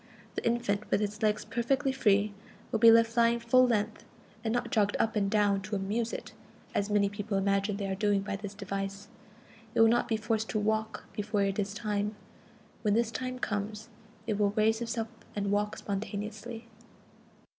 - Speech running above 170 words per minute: Yes, average, 185 wpm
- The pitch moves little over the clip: Yes, narrow, 2.1 semitones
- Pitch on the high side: Yes, high, 210 Hz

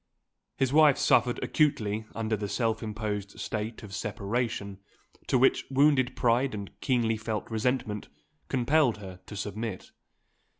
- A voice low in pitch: Yes, low, 115 Hz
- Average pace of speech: No, slow, 130 wpm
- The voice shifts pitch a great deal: No, average, 3.4 semitones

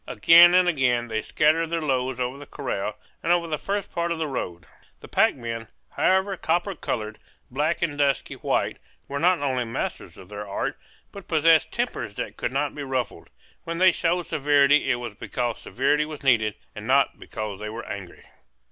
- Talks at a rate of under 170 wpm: No, average, 190 wpm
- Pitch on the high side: No, medium, 140 Hz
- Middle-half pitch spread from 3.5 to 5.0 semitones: No, wide, 5.6 semitones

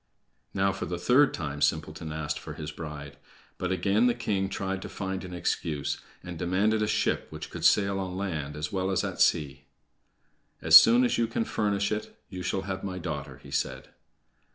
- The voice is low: Yes, very low, 95 Hz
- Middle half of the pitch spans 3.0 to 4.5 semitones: Yes, average, 4.1 semitones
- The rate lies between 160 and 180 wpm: No, average, 195 wpm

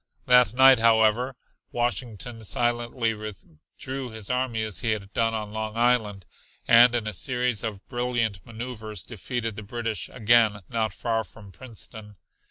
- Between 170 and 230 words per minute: No, average, 145 wpm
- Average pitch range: No, narrow, 2.2 semitones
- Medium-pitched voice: No, low, 115 Hz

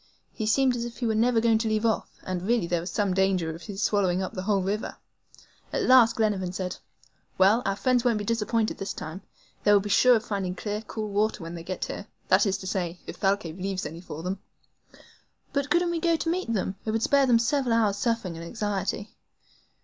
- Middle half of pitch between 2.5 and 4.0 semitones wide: Yes, average, 3.6 semitones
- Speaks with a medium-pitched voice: No, high, 205 Hz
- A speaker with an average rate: No, fast, 225 wpm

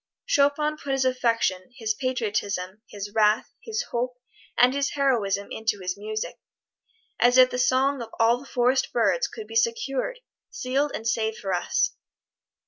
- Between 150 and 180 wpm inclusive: Yes, average, 155 wpm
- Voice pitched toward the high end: Yes, high, 245 Hz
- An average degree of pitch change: Yes, average, 4.3 semitones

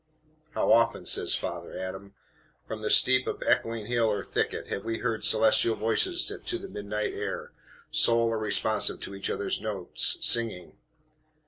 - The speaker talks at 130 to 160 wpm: Yes, average, 155 wpm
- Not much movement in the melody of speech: Yes, narrow, 2.1 semitones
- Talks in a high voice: No, low, 110 Hz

